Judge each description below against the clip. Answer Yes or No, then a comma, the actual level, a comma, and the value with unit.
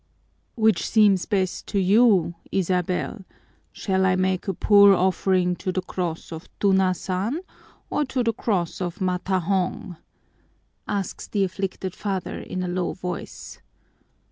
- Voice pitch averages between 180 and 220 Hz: Yes, high, 190 Hz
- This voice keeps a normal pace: No, slow, 130 wpm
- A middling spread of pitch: No, narrow, 1.8 semitones